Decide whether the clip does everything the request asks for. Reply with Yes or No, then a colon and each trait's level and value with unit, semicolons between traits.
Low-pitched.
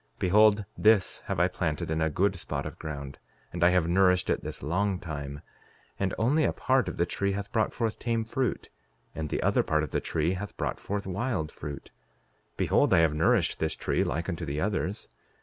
Yes: very low, 90 Hz